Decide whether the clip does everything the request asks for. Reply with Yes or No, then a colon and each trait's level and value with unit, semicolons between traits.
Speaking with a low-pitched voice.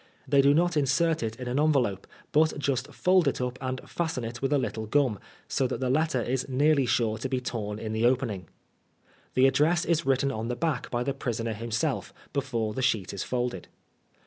Yes: low, 130 Hz